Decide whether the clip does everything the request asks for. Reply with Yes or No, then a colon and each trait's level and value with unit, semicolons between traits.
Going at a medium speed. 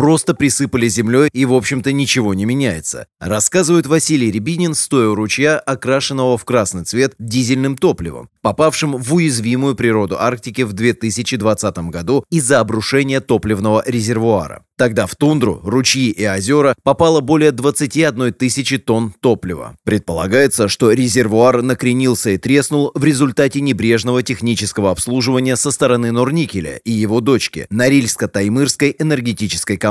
Yes: average, 130 wpm